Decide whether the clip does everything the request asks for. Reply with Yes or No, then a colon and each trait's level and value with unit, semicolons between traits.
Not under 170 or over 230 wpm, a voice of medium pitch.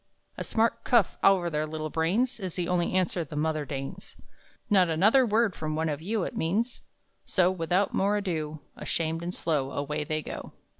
Yes: average, 185 wpm; medium, 170 Hz